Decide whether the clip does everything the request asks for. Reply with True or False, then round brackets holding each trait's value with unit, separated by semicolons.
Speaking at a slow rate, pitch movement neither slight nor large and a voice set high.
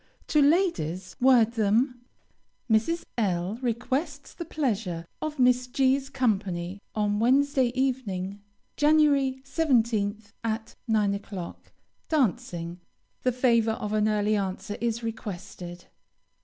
True (115 wpm; 4.7 semitones; 230 Hz)